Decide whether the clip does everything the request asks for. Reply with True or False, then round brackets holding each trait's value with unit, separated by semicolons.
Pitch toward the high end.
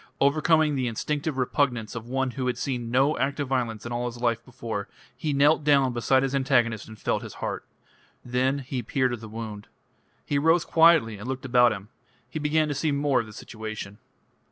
False (130 Hz)